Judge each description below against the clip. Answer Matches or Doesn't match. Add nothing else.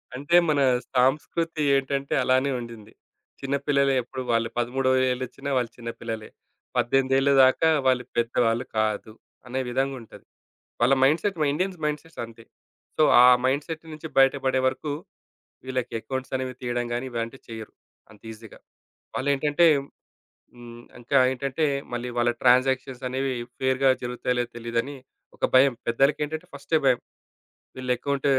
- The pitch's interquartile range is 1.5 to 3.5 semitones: Matches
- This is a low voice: Matches